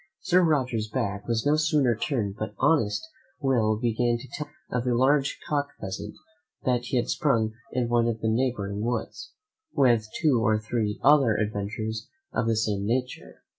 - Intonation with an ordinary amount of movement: Yes, average, 3.5 semitones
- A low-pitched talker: Yes, low, 120 Hz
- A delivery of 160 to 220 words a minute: Yes, average, 170 wpm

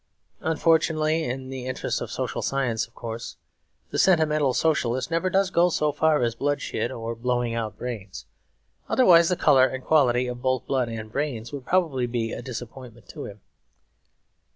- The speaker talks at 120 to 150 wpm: No, average, 165 wpm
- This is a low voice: Yes, low, 130 Hz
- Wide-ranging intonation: No, average, 4.7 semitones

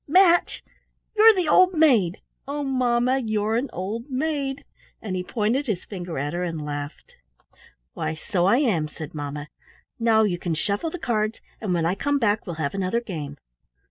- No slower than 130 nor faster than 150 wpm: No, average, 175 wpm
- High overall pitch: Yes, high, 215 Hz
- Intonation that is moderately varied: No, wide, 7.5 semitones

